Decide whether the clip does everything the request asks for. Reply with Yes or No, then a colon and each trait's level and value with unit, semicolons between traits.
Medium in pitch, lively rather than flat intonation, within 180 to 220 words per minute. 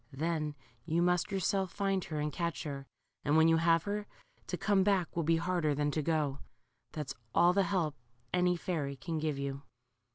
No: medium, 165 Hz; average, 3.2 semitones; average, 190 wpm